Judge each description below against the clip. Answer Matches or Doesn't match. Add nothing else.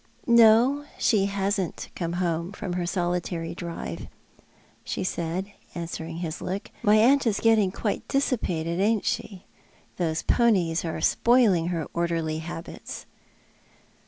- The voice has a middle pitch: Matches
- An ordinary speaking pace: Doesn't match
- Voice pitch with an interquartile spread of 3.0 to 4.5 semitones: Matches